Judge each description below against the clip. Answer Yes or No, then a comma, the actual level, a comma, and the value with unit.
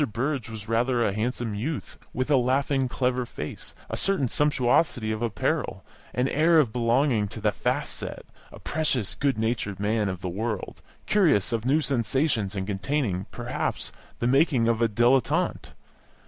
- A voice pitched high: No, low, 120 Hz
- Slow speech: No, average, 160 wpm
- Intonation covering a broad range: No, average, 3.9 semitones